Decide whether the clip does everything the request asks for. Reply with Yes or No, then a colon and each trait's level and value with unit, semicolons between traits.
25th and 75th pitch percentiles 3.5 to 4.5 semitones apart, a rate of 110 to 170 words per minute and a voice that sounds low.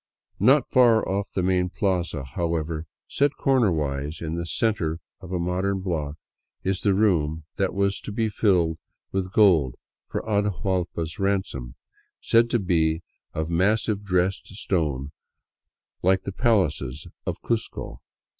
Yes: average, 3.9 semitones; slow, 135 wpm; very low, 90 Hz